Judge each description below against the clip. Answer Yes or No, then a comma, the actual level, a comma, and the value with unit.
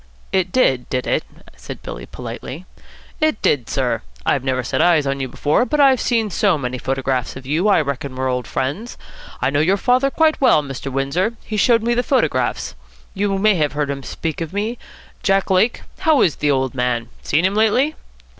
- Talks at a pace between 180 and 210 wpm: Yes, average, 200 wpm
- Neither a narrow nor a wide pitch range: No, wide, 8.3 semitones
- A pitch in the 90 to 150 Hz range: No, medium, 160 Hz